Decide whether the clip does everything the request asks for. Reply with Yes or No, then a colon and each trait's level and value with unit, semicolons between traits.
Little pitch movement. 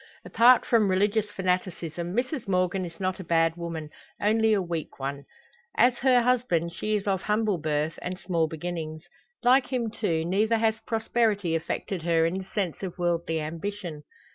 No: average, 4.7 semitones